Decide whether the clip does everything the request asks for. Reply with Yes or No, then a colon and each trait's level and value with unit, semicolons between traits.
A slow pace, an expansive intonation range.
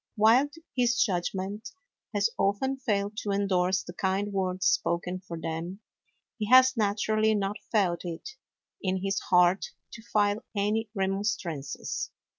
No: slow, 130 wpm; average, 2.7 semitones